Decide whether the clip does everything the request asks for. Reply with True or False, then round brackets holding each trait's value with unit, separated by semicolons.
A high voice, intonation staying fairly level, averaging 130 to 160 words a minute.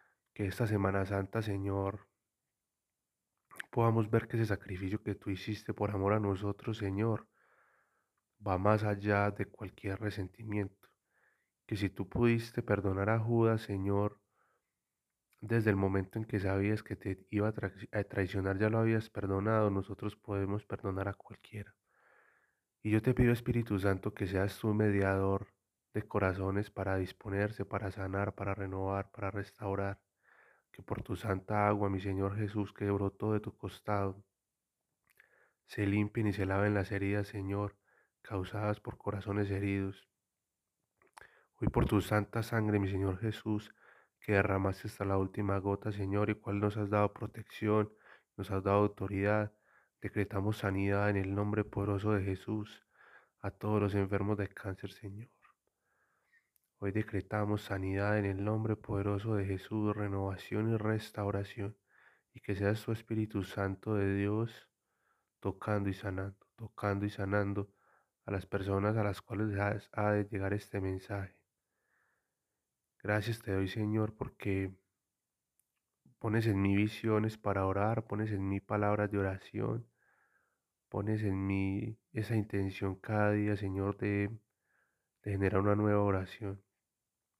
False (100 Hz; 1.5 semitones; 140 wpm)